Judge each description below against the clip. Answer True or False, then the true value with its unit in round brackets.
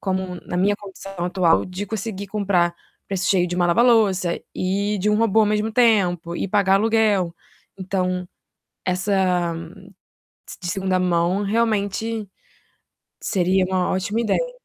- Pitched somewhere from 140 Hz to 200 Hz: True (190 Hz)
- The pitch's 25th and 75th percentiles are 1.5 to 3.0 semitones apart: True (2.5 semitones)